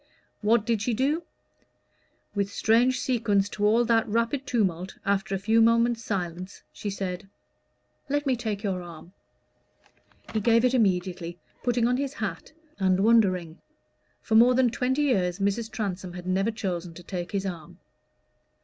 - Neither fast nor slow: Yes, average, 155 wpm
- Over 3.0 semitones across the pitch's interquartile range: Yes, average, 4.1 semitones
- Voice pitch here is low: No, high, 210 Hz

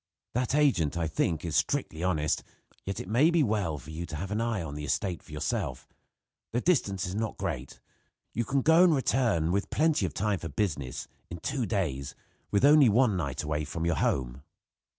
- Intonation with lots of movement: Yes, wide, 7.5 semitones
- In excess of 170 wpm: Yes, average, 200 wpm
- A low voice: Yes, very low, 95 Hz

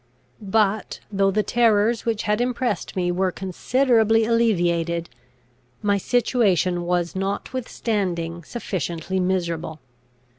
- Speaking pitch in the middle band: No, high, 195 Hz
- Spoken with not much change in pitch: No, average, 4.3 semitones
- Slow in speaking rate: Yes, slow, 100 wpm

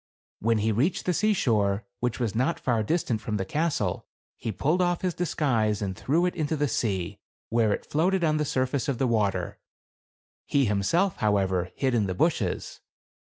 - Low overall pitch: Yes, low, 120 Hz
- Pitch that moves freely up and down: Yes, wide, 7.0 semitones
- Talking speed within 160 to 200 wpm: Yes, average, 185 wpm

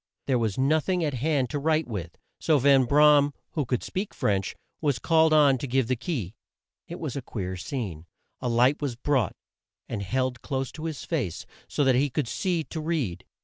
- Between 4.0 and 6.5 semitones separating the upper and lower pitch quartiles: Yes, average, 4.3 semitones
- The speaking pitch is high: No, low, 135 Hz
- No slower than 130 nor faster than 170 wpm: No, fast, 205 wpm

